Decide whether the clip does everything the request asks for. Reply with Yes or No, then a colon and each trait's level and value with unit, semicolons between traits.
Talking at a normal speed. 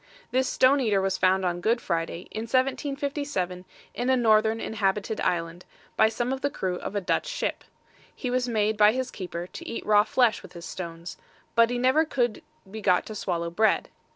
Yes: average, 195 wpm